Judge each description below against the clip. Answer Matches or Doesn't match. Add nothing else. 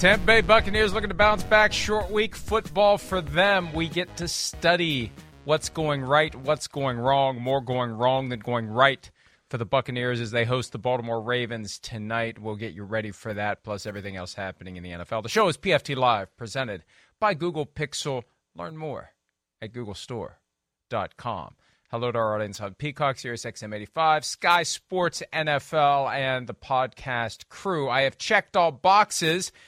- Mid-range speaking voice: Doesn't match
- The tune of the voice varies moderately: Doesn't match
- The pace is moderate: Matches